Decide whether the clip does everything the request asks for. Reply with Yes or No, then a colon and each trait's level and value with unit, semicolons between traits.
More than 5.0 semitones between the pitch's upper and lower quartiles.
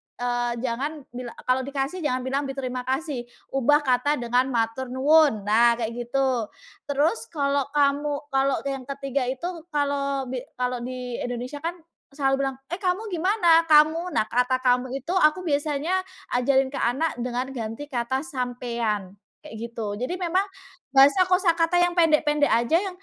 No: average, 3.5 semitones